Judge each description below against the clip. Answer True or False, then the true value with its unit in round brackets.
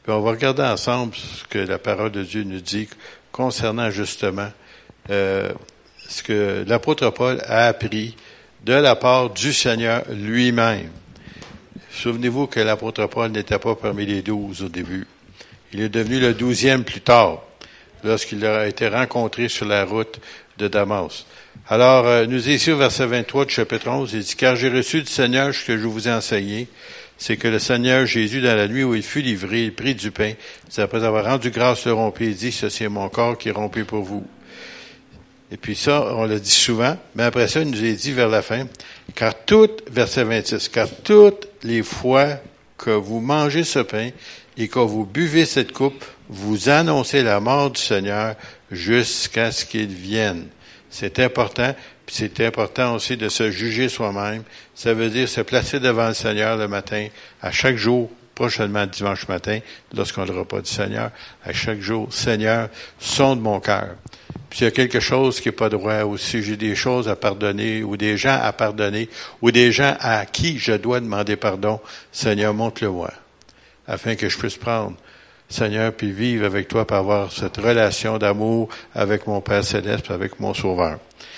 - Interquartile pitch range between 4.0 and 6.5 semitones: False (2.9 semitones)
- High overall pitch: False (115 Hz)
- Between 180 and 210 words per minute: True (185 wpm)